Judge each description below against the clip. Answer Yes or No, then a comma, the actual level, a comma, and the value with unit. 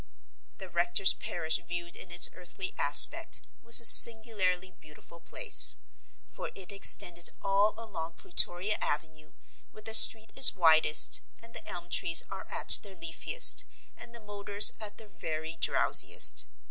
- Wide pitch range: No, average, 4.2 semitones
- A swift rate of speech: No, average, 145 wpm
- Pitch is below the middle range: No, medium, 185 Hz